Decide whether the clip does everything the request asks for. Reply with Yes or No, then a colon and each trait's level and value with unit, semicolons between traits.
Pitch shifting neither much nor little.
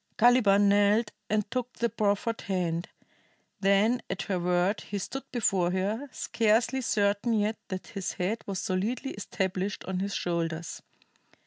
Yes: average, 3.2 semitones